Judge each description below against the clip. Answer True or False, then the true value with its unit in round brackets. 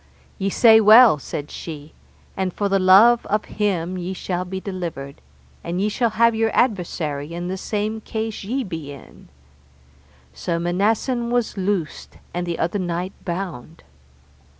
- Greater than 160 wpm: False (150 wpm)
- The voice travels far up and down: False (4.2 semitones)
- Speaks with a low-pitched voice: False (190 Hz)